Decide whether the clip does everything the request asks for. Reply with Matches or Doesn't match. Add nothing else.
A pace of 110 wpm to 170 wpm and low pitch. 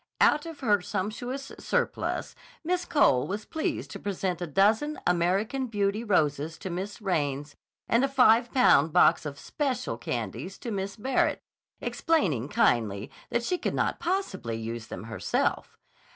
Doesn't match